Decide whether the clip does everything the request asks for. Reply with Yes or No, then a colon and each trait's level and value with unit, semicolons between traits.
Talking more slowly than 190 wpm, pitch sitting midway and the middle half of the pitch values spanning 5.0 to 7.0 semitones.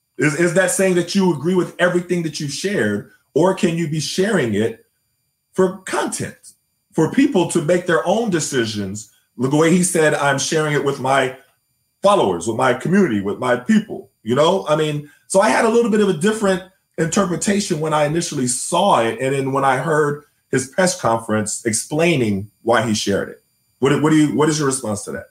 No: average, 200 wpm; medium, 155 Hz; wide, 5.5 semitones